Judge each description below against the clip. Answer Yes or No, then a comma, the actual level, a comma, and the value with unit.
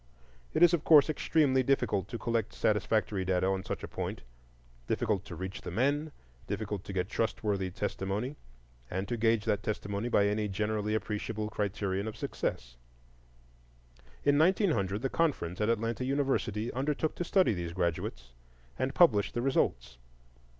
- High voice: No, low, 105 Hz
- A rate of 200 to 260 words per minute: No, average, 145 wpm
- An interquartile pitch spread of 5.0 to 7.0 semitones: Yes, wide, 5.4 semitones